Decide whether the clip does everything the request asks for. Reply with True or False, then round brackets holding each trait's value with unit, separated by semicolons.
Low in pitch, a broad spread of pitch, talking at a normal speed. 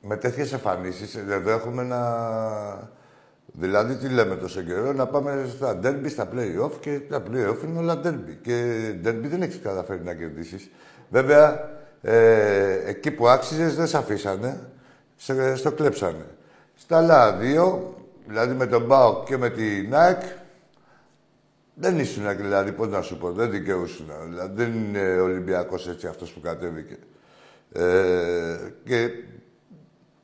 True (115 Hz; 6.7 semitones; 140 wpm)